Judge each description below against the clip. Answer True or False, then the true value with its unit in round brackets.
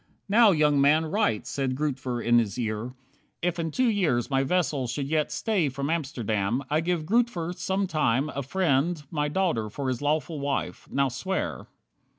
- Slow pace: False (165 wpm)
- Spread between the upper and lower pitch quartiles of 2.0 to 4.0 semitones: False (4.9 semitones)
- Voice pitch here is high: False (150 Hz)